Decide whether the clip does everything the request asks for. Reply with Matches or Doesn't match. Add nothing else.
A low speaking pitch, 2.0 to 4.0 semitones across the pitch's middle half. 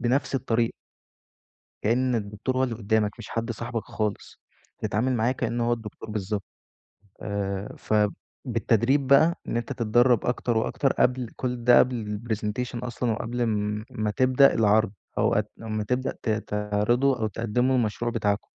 Matches